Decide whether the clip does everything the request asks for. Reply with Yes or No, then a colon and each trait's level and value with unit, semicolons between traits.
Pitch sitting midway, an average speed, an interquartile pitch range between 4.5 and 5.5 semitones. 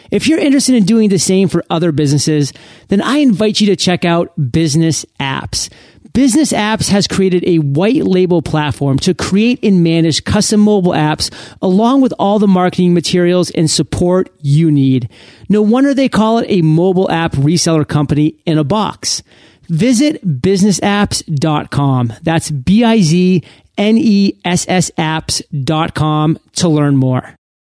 Yes: medium, 175 Hz; average, 155 wpm; average, 5.1 semitones